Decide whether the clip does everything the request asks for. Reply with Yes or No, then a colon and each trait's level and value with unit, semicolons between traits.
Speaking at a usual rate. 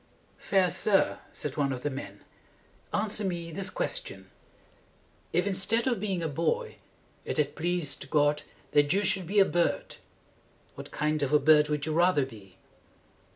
Yes: average, 160 wpm